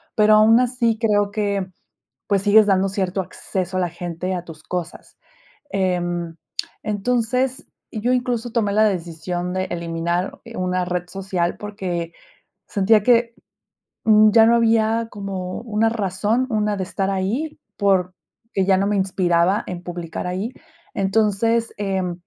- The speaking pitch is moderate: No, high, 195 Hz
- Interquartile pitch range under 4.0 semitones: Yes, average, 3.5 semitones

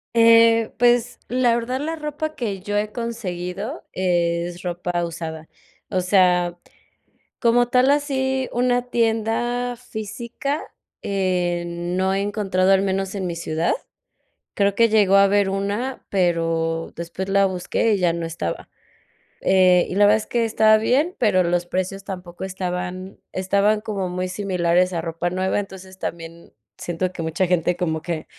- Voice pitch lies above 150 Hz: Yes, high, 190 Hz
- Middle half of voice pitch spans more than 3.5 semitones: Yes, average, 4.3 semitones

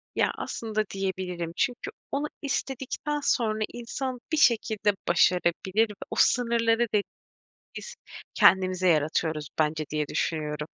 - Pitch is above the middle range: Yes, high, 205 Hz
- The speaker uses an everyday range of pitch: No, wide, 5.8 semitones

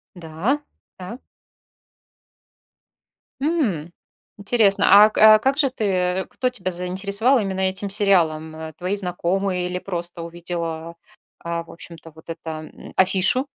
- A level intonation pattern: No, average, 3.3 semitones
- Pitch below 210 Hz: Yes, medium, 185 Hz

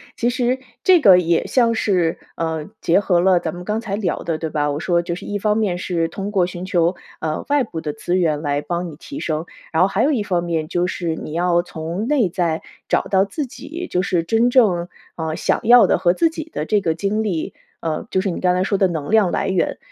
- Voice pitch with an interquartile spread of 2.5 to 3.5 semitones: No, average, 4.2 semitones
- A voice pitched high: No, medium, 180 Hz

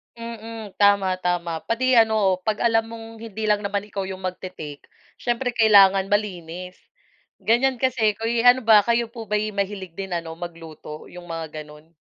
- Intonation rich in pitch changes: No, average, 3.8 semitones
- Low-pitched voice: No, high, 205 Hz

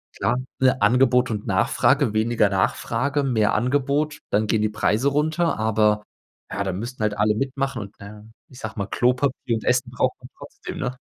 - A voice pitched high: No, low, 120 Hz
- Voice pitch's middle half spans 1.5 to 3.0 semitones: No, average, 3.8 semitones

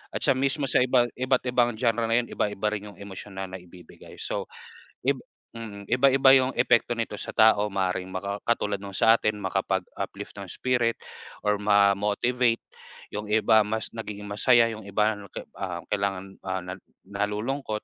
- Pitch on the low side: Yes, low, 105 Hz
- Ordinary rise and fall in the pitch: Yes, average, 3.0 semitones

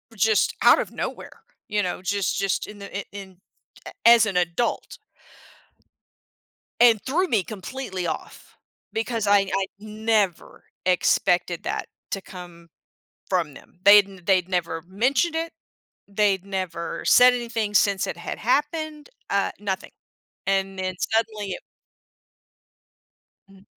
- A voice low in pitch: No, high, 200 Hz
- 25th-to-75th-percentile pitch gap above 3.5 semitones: No, average, 3.2 semitones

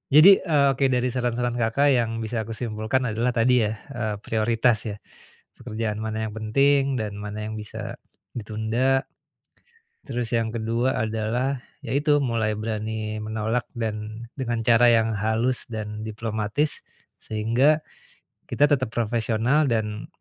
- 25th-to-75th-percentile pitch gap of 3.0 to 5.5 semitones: No, narrow, 2.4 semitones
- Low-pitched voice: Yes, low, 115 Hz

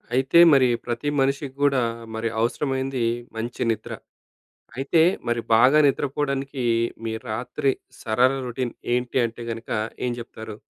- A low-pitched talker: Yes, low, 130 Hz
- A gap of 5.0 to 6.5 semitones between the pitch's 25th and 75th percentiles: No, average, 2.7 semitones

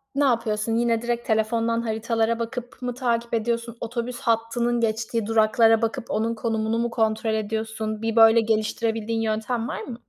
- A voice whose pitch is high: Yes, high, 230 Hz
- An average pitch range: No, narrow, 1.1 semitones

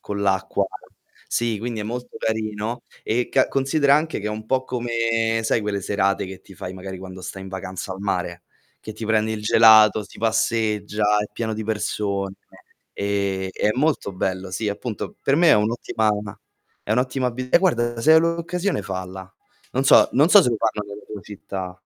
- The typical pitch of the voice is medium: No, low, 110 Hz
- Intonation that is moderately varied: Yes, average, 3.6 semitones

